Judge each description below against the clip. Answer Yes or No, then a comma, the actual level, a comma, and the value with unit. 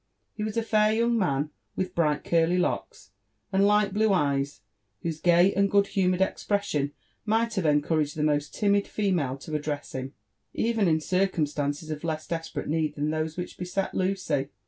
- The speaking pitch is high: No, medium, 170 Hz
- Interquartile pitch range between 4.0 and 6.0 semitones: Yes, average, 4.9 semitones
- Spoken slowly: No, average, 175 wpm